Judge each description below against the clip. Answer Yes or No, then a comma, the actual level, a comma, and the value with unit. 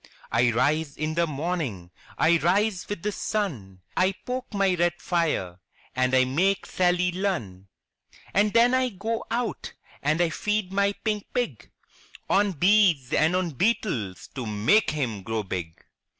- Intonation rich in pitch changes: Yes, wide, 7.9 semitones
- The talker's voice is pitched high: No, medium, 175 Hz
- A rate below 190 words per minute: Yes, average, 150 wpm